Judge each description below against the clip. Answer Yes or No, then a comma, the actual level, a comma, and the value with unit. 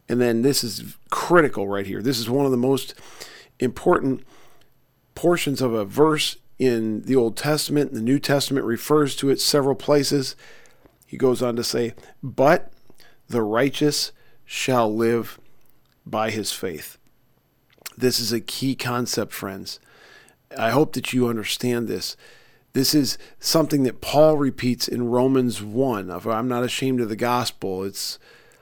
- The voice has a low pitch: Yes, low, 125 Hz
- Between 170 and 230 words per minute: No, average, 150 wpm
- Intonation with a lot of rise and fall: No, average, 3.0 semitones